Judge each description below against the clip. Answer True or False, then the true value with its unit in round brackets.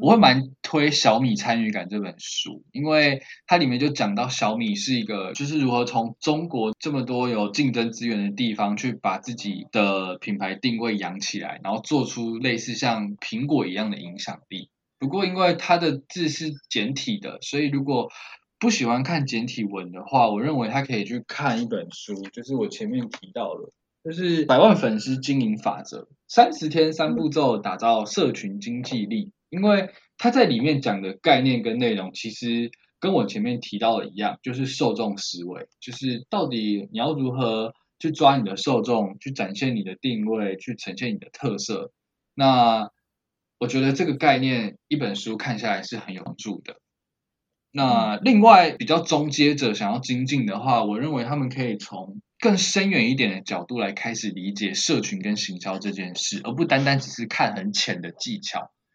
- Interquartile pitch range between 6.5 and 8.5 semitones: True (6.8 semitones)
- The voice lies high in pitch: False (130 Hz)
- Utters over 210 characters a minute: True (275 characters per minute)